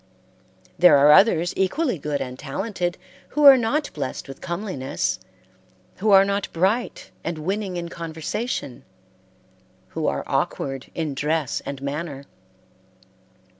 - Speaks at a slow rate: Yes, slow, 125 wpm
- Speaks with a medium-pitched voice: Yes, medium, 170 Hz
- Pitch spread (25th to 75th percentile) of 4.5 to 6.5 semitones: Yes, wide, 5.6 semitones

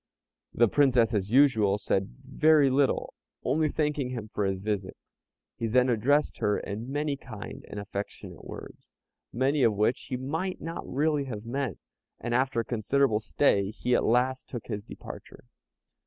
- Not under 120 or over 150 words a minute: No, average, 160 wpm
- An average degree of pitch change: Yes, average, 4.7 semitones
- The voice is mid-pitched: No, low, 125 Hz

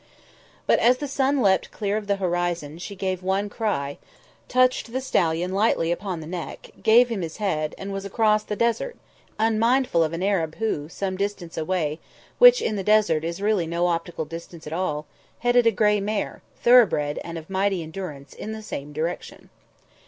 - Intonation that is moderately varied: Yes, average, 4.6 semitones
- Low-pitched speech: No, high, 195 Hz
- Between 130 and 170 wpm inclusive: No, average, 180 wpm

